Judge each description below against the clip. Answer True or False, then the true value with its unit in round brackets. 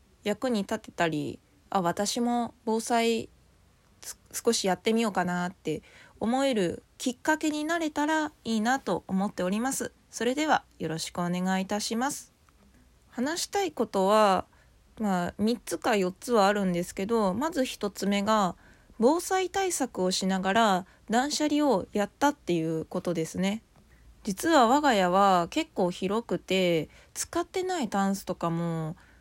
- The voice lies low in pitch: False (210 Hz)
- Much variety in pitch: True (5.9 semitones)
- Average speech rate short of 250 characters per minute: False (275 characters per minute)